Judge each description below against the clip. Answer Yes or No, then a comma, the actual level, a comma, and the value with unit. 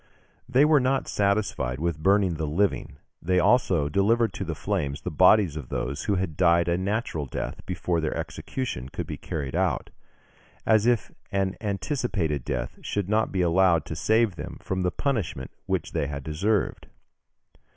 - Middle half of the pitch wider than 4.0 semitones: Yes, average, 5.2 semitones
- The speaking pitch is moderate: No, very low, 90 Hz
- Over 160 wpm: Yes, average, 170 wpm